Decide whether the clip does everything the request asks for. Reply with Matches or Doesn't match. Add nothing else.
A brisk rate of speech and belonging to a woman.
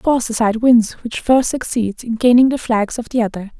Matches